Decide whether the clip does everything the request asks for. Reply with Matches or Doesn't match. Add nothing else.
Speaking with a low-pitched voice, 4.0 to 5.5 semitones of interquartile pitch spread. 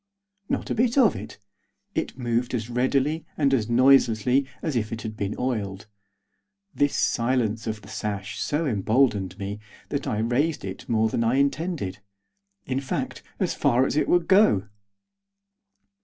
Matches